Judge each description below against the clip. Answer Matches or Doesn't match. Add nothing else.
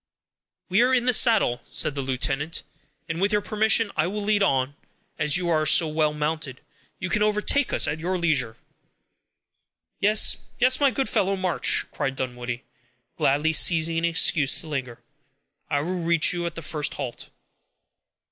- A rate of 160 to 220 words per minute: Matches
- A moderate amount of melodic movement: Doesn't match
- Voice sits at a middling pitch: Matches